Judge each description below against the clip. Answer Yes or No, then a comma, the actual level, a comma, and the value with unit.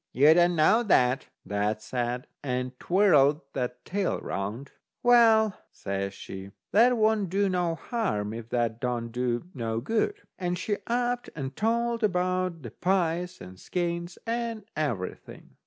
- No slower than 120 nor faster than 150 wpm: Yes, average, 145 wpm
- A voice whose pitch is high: No, medium, 170 Hz